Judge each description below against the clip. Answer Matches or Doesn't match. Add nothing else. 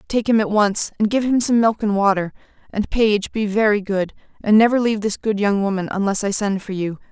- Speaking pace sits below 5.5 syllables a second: Doesn't match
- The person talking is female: Matches